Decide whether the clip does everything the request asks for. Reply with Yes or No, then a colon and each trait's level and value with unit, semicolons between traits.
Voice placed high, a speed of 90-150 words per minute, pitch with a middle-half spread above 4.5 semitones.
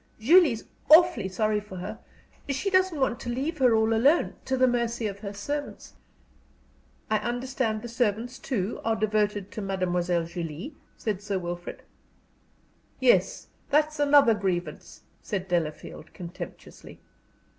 Yes: high, 220 Hz; slow, 135 wpm; wide, 5.4 semitones